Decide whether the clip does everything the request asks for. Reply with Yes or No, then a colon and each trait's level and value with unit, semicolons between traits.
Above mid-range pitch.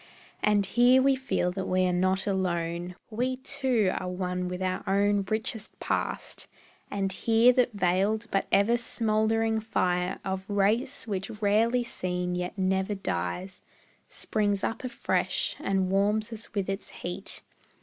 Yes: high, 200 Hz